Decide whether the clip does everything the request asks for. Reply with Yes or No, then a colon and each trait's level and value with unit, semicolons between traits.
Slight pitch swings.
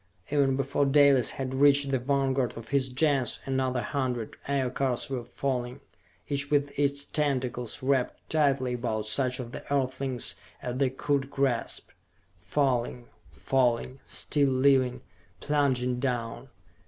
Yes: narrow, 2.0 semitones